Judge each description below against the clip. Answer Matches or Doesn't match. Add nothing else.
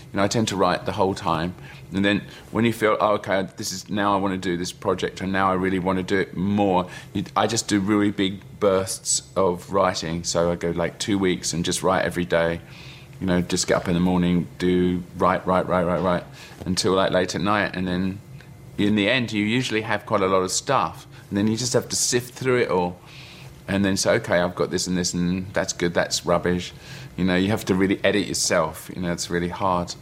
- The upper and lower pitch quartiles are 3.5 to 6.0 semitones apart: Doesn't match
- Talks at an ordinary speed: Doesn't match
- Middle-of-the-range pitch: Doesn't match